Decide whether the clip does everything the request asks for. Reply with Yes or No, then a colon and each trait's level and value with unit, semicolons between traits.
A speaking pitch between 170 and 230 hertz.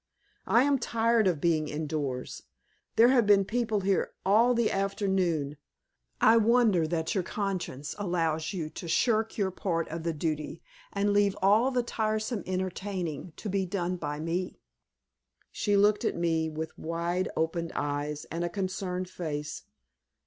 Yes: medium, 185 Hz